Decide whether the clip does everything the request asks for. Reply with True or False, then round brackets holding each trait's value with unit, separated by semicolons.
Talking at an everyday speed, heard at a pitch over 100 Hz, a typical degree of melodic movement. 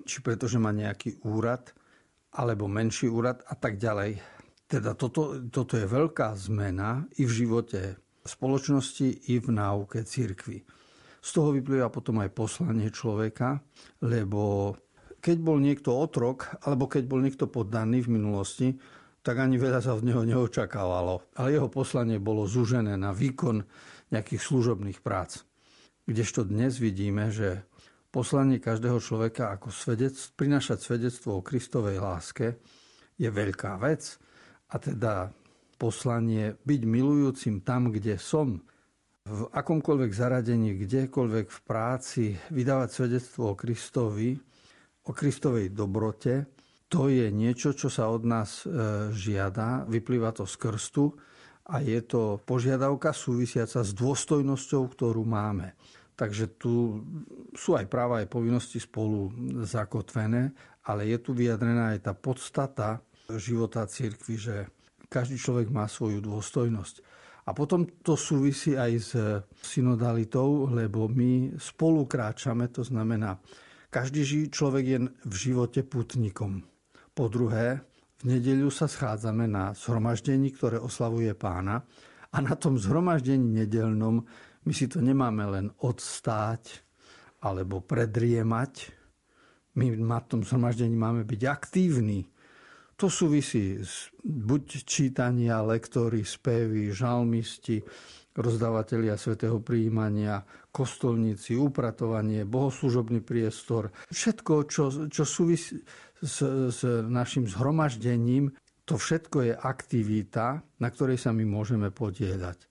True (120 wpm; 120 Hz; 3.4 semitones)